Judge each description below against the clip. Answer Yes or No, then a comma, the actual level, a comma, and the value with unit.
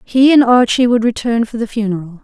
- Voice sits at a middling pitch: No, high, 230 Hz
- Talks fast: Yes, fast, 215 wpm